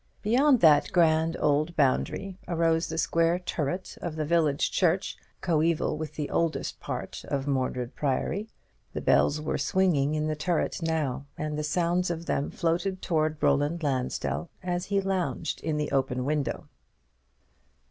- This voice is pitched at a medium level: Yes, medium, 160 Hz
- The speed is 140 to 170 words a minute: Yes, average, 150 wpm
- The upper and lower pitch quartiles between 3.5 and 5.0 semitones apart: No, average, 2.8 semitones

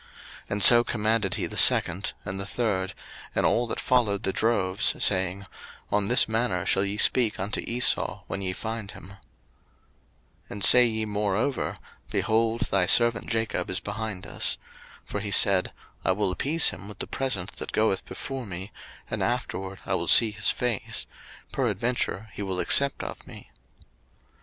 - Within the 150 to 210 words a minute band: Yes, average, 165 wpm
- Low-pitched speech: Yes, low, 105 Hz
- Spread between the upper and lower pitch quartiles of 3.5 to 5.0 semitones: No, average, 3.1 semitones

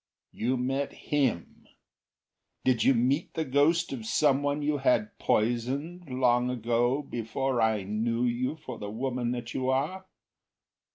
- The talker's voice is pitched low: Yes, low, 130 Hz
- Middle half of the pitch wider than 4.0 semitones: No, average, 3.2 semitones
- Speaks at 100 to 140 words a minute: Yes, slow, 135 wpm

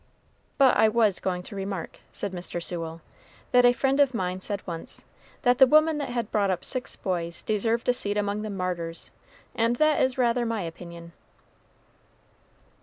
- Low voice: No, high, 205 Hz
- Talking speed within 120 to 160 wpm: No, average, 175 wpm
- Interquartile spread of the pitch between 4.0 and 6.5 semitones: Yes, wide, 5.4 semitones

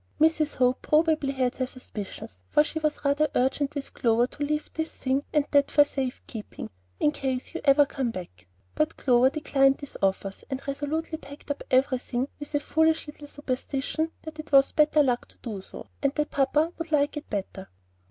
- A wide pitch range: No, average, 2.9 semitones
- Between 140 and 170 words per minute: No, average, 190 wpm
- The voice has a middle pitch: No, very high, 280 Hz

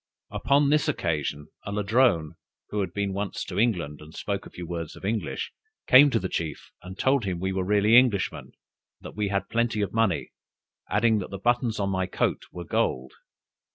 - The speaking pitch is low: Yes, low, 100 Hz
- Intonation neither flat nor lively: Yes, average, 4.3 semitones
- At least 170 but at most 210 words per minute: Yes, average, 195 wpm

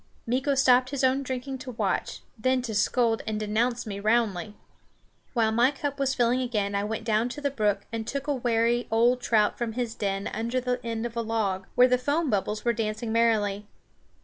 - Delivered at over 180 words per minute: Yes, average, 200 wpm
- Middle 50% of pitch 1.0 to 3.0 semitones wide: Yes, average, 2.7 semitones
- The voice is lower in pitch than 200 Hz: No, high, 235 Hz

